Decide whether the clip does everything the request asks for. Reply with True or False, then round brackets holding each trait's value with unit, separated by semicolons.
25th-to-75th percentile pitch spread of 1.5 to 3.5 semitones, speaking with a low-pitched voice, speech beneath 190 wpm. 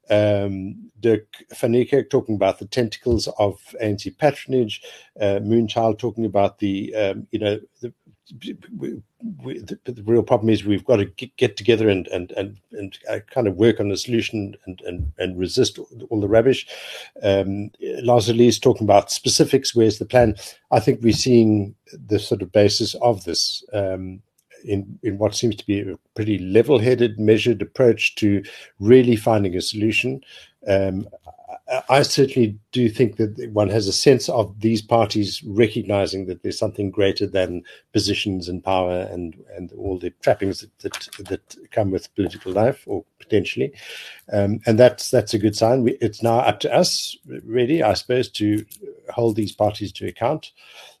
True (3.2 semitones; 110 Hz; 170 wpm)